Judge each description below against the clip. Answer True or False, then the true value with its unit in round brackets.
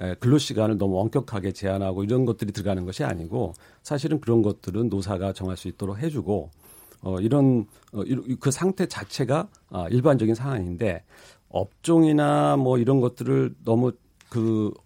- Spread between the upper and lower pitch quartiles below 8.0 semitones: True (5.2 semitones)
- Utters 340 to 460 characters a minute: False (315 characters per minute)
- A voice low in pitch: True (110 Hz)